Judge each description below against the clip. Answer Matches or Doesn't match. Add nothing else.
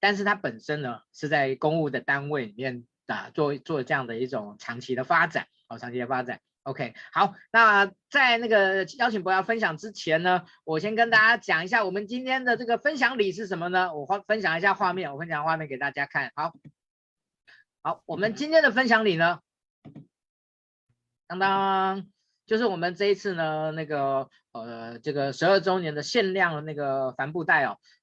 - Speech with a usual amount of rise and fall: Doesn't match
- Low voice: Doesn't match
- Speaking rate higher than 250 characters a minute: Matches